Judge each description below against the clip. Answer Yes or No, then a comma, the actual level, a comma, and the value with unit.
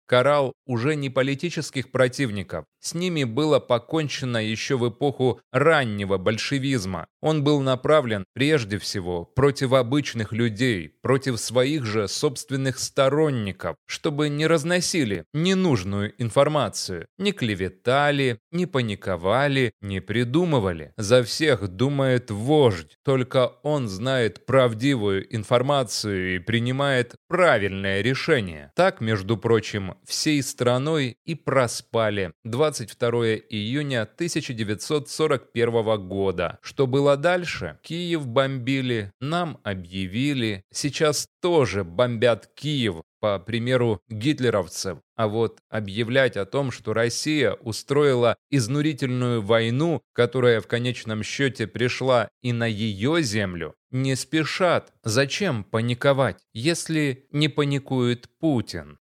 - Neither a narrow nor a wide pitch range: Yes, average, 4.5 semitones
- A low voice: Yes, low, 125 Hz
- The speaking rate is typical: No, slow, 105 wpm